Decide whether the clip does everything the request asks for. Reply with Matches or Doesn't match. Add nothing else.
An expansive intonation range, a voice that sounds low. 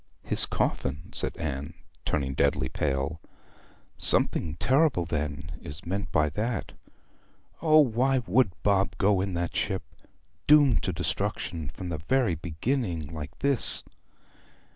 Matches